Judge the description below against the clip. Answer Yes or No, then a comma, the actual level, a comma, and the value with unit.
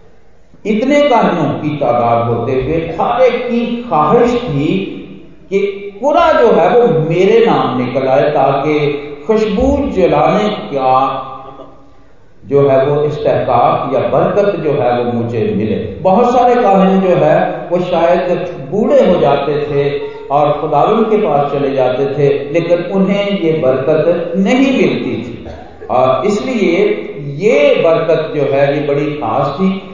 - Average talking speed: Yes, average, 140 wpm